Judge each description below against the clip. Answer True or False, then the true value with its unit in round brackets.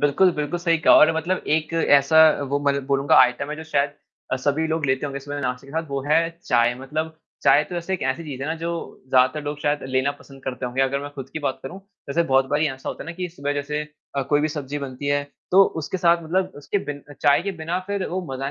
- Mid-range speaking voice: True (145 Hz)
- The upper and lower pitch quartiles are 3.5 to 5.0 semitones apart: False (2.8 semitones)